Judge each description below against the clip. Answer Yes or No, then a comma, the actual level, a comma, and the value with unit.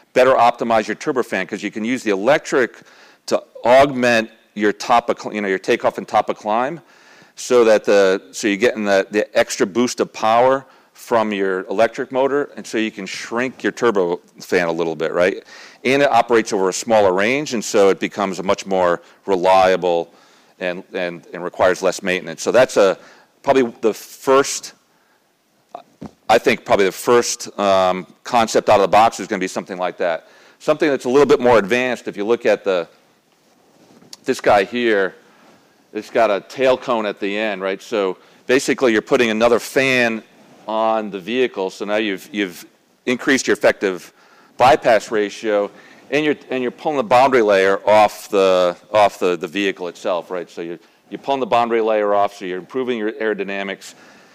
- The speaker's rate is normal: Yes, average, 185 wpm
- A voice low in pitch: Yes, low, 105 Hz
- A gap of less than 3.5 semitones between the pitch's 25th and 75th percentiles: No, average, 3.9 semitones